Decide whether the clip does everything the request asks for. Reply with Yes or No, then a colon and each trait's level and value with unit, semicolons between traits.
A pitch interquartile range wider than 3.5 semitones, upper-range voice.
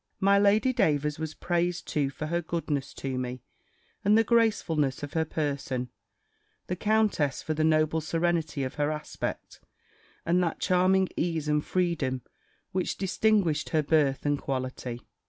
No: average, 3.9 semitones; medium, 160 Hz